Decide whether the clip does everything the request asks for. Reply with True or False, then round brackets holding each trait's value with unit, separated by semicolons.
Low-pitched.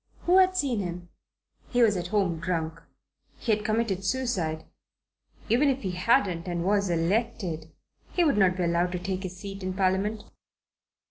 False (190 Hz)